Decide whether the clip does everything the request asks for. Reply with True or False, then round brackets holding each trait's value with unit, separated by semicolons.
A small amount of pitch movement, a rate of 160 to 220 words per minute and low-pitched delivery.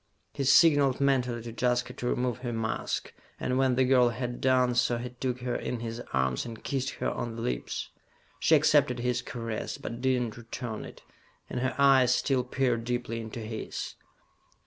True (1.8 semitones; 185 wpm; 125 Hz)